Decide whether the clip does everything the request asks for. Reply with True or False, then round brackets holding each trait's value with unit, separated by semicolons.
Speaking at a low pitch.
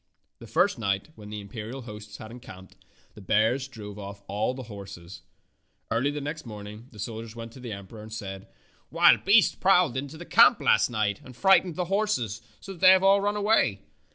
True (115 Hz)